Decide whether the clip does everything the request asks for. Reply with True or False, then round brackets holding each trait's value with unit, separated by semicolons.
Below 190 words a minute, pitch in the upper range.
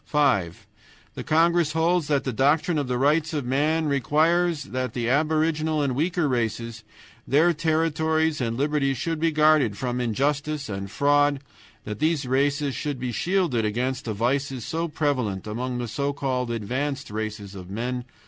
False (165 wpm; 140 Hz)